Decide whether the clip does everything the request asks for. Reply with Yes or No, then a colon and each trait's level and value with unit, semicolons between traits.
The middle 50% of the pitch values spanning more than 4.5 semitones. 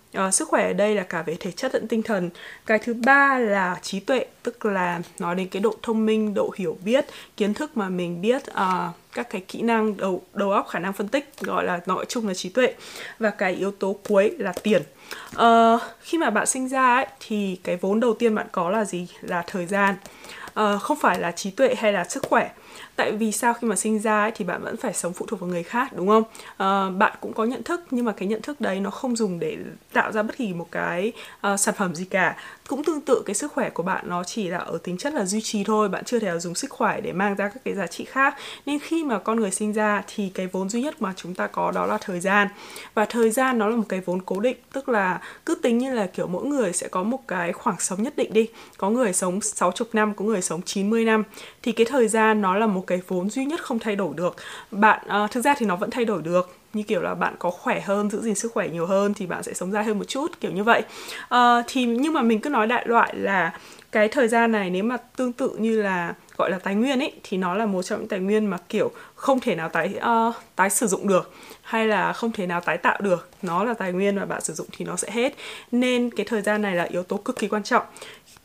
No: average, 3.8 semitones